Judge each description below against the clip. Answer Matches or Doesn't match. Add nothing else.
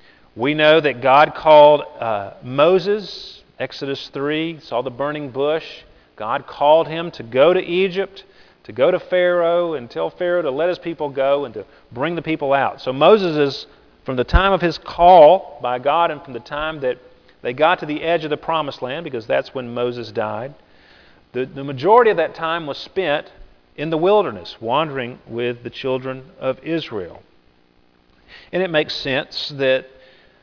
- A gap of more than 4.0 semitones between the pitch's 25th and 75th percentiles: Matches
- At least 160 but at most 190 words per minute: Matches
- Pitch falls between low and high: Matches